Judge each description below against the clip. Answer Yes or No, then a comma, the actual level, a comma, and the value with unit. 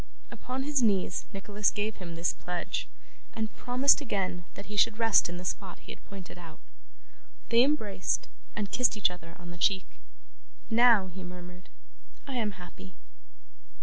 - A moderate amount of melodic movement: Yes, average, 4.2 semitones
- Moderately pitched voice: No, high, 200 Hz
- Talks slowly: No, average, 160 wpm